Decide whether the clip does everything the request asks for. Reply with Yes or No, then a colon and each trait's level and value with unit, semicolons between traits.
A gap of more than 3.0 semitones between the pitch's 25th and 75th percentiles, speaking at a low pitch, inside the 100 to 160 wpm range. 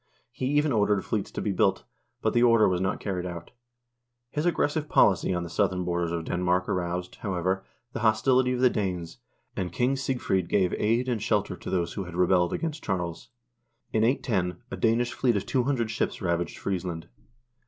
No: wide, 5.4 semitones; very low, 95 Hz; average, 185 wpm